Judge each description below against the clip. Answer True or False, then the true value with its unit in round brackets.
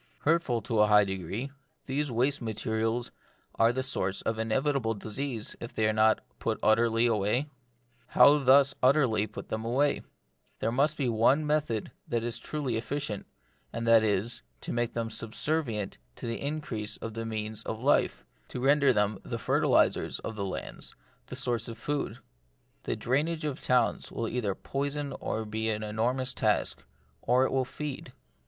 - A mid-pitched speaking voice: False (115 Hz)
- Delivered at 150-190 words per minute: True (170 wpm)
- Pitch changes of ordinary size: True (3.9 semitones)